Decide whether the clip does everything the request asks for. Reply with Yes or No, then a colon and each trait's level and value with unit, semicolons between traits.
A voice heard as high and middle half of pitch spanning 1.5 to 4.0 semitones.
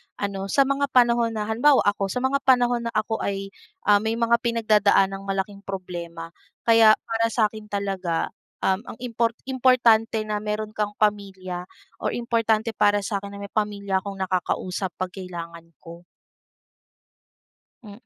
Yes: high, 210 Hz; average, 2.8 semitones